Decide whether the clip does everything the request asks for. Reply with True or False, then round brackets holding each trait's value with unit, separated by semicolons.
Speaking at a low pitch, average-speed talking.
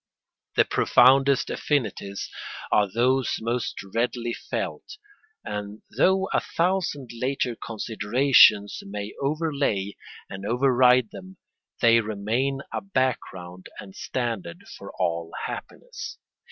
False (120 Hz; 100 wpm)